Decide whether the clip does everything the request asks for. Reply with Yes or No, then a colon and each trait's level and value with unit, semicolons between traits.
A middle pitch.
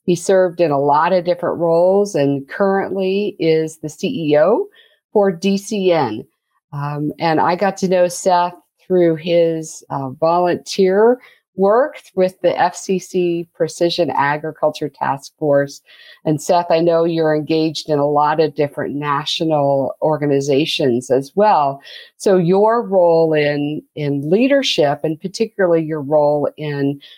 Yes: medium, 165 Hz